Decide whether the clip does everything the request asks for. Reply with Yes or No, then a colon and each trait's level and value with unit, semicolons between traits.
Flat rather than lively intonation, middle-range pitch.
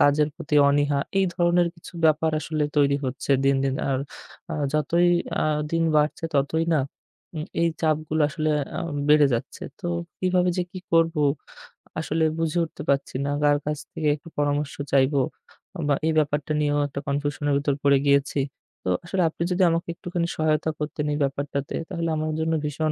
Yes: narrow, 2.3 semitones; medium, 150 Hz